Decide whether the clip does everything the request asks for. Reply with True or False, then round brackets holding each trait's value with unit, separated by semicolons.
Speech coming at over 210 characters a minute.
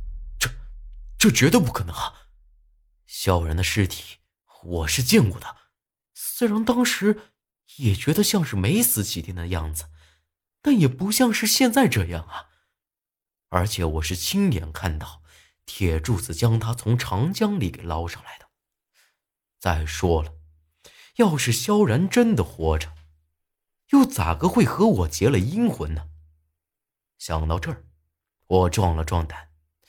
False (195 characters per minute)